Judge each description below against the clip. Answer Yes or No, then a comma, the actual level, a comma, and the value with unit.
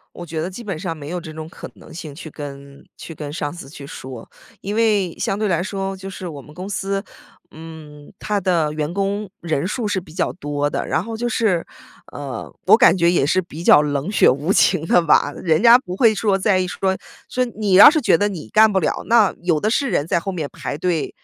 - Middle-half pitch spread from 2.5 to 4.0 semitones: No, average, 4.5 semitones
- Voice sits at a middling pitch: Yes, medium, 175 Hz